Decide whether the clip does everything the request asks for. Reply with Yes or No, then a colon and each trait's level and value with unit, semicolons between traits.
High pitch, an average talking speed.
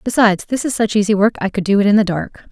No: high, 210 Hz; fast, 310 wpm